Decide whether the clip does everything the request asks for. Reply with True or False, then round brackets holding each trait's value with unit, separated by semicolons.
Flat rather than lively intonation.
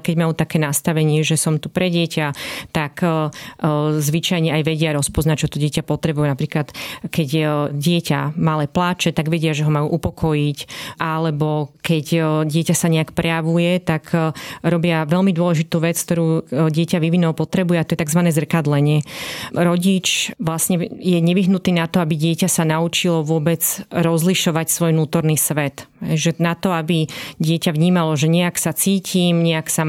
True (1.8 semitones)